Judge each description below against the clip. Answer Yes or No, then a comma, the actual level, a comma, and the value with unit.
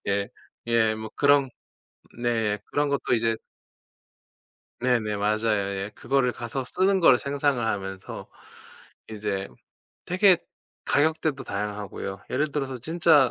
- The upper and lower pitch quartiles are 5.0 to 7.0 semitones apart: Yes, average, 5.3 semitones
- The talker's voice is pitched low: Yes, low, 120 Hz